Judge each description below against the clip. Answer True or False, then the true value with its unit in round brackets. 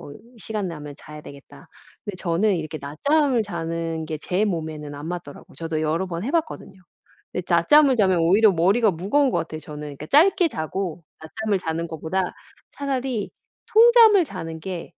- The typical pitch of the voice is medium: True (180 Hz)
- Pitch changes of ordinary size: False (5.7 semitones)